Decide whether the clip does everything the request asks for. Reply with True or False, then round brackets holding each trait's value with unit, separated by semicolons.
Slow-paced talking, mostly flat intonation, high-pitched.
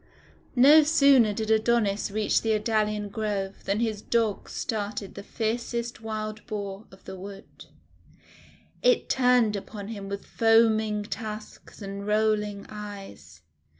True (125 wpm; 1.8 semitones; 215 Hz)